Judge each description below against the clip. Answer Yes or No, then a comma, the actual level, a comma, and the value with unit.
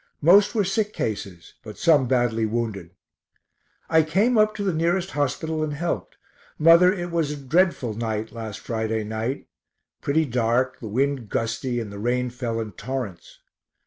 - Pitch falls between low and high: No, low, 130 Hz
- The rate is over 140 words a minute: Yes, average, 160 wpm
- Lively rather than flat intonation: Yes, wide, 6.7 semitones